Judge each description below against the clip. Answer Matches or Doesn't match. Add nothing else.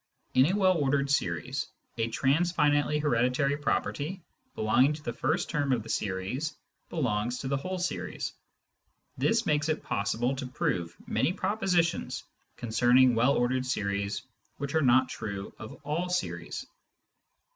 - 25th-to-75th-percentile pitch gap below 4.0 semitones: Doesn't match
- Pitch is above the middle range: Doesn't match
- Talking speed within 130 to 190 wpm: Matches